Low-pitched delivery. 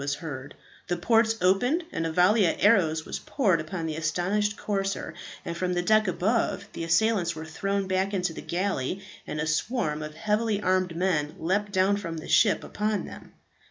No: medium, 185 Hz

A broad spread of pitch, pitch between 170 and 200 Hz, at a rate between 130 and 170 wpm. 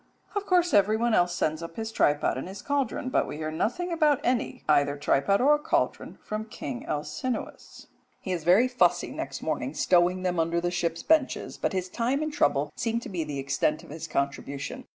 No: wide, 8.2 semitones; medium, 185 Hz; average, 195 wpm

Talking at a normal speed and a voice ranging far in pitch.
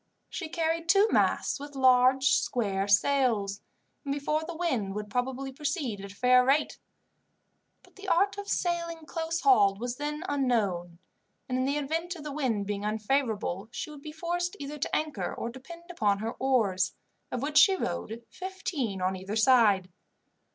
Yes: average, 170 wpm; wide, 7.0 semitones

